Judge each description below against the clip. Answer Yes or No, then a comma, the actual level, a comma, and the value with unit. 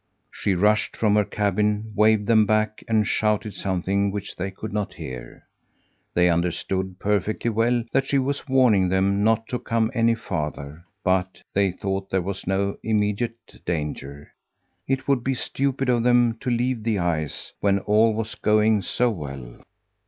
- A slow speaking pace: No, average, 160 wpm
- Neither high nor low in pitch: No, low, 105 Hz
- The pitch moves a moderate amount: Yes, average, 3.3 semitones